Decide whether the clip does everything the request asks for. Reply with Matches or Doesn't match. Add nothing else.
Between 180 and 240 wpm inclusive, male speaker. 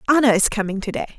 Doesn't match